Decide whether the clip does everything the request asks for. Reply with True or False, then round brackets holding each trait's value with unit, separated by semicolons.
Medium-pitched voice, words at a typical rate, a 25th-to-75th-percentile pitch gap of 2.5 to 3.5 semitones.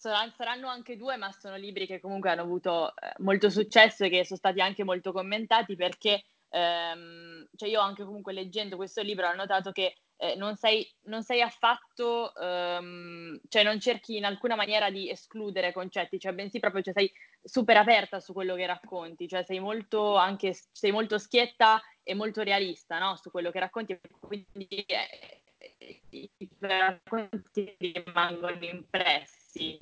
False (195 Hz; 160 wpm; 2.9 semitones)